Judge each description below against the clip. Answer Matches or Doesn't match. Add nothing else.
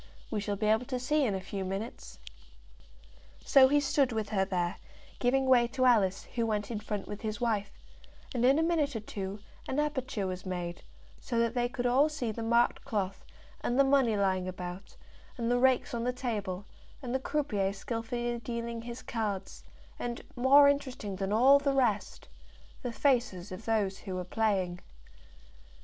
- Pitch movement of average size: Matches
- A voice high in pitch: Matches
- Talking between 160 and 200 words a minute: Matches